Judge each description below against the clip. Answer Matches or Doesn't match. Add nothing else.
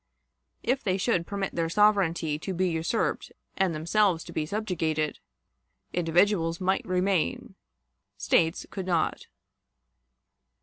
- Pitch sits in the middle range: Matches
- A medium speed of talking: Doesn't match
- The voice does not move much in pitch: Doesn't match